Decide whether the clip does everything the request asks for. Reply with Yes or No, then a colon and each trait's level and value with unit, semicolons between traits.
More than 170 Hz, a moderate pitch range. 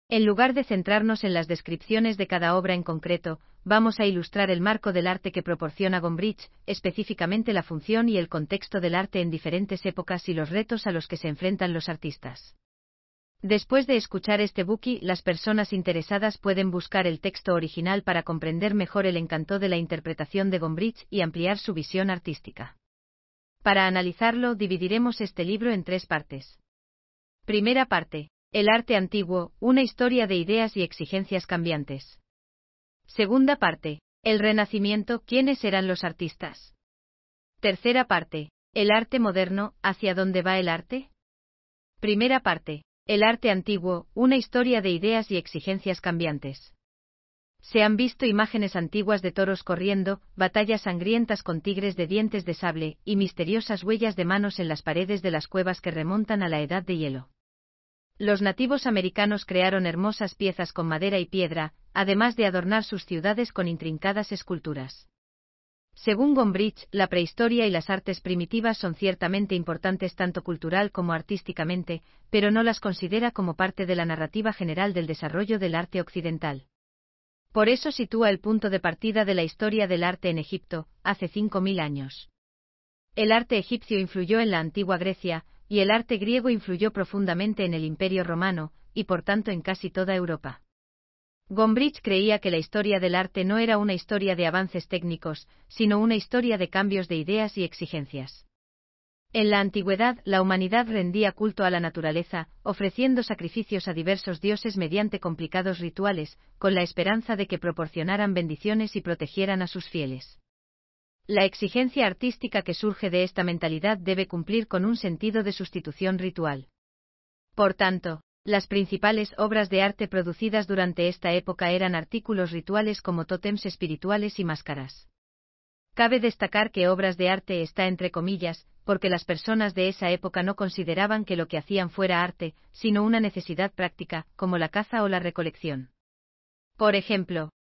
Yes: high, 190 Hz; average, 3.6 semitones